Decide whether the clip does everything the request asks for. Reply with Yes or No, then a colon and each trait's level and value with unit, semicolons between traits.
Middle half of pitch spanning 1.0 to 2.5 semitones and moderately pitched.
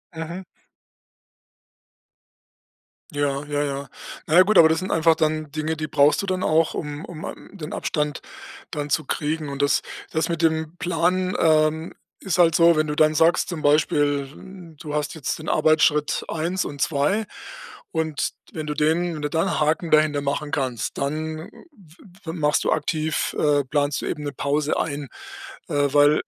Yes: narrow, 1.8 semitones; medium, 155 Hz